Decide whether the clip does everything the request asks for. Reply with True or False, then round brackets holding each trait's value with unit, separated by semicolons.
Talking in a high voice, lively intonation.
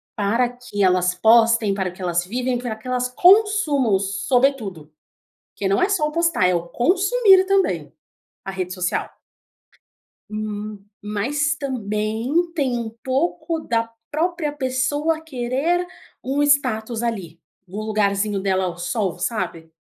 True (235 Hz; 6.6 semitones)